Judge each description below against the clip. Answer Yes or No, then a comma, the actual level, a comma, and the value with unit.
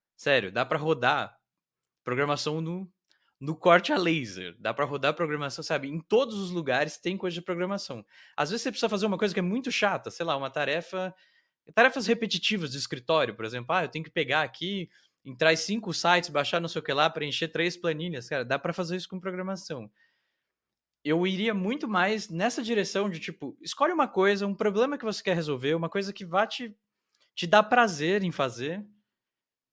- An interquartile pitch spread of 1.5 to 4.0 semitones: No, average, 4.7 semitones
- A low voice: No, medium, 175 Hz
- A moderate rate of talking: No, fast, 195 wpm